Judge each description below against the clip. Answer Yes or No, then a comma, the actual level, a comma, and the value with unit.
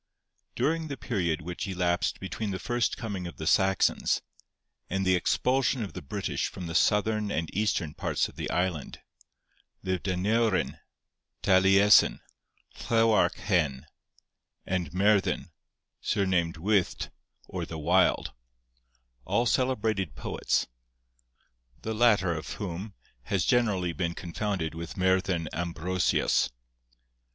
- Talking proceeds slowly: Yes, slow, 115 wpm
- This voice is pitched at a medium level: No, very low, 95 Hz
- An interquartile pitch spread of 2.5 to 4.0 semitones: Yes, average, 3.6 semitones